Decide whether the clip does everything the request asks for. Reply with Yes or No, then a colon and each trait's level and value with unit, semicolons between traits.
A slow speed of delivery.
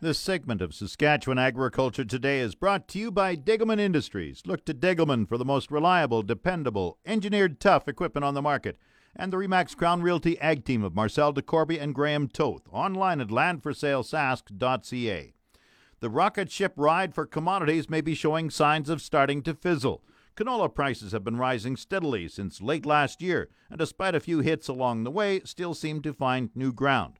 No: average, 180 wpm